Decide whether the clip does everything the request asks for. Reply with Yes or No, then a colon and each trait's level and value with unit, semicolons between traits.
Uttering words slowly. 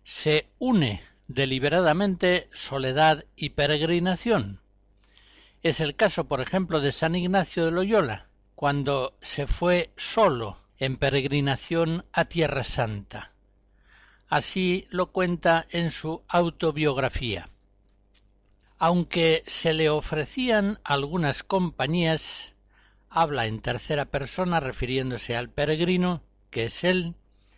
Yes: slow, 100 wpm